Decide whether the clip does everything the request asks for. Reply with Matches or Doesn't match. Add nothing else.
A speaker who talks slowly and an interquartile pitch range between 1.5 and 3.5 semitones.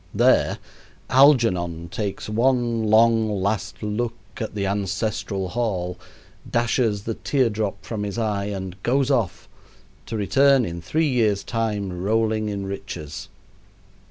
Matches